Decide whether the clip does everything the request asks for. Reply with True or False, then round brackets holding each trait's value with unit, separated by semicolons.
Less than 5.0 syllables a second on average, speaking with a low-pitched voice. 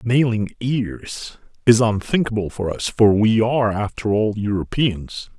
True (4.1 syllables/s; 110 Hz)